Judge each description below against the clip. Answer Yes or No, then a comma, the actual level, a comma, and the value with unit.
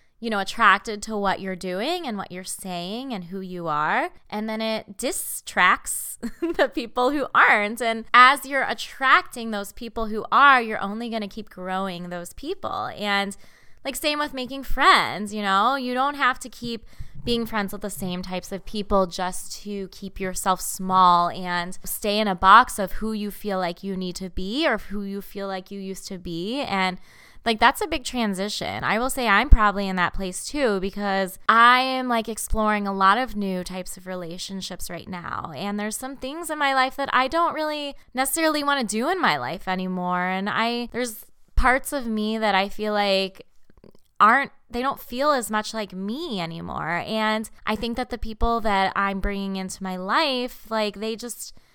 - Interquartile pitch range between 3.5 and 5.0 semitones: Yes, average, 4.6 semitones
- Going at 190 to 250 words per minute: Yes, average, 195 wpm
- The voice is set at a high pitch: Yes, high, 210 Hz